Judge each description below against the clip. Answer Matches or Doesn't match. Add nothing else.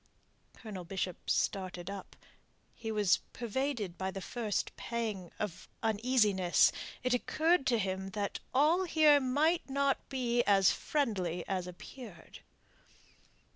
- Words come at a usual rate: Doesn't match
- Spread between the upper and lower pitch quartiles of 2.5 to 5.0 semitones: Doesn't match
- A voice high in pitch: Matches